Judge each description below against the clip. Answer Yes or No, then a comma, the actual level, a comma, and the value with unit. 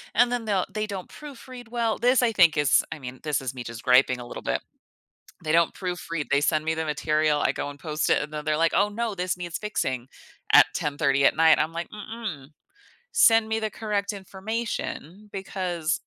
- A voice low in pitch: No, medium, 170 Hz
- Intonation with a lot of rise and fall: Yes, wide, 6.1 semitones